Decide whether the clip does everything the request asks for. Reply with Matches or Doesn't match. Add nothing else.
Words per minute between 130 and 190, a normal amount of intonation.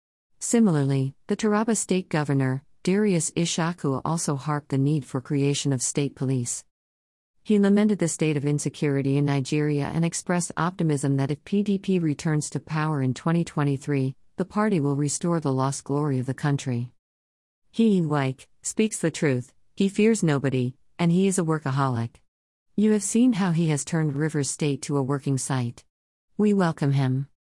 Matches